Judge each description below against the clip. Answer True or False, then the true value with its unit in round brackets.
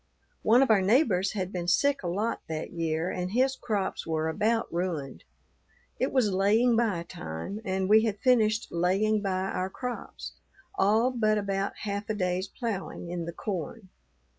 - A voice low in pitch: False (200 Hz)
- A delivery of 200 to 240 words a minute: False (165 wpm)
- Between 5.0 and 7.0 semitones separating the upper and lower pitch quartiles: False (3.8 semitones)